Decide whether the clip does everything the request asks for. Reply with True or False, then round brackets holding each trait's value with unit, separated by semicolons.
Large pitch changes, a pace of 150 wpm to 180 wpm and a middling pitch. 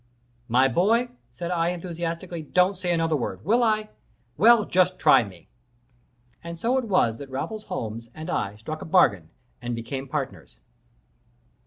True (6.8 semitones; 155 wpm; 165 Hz)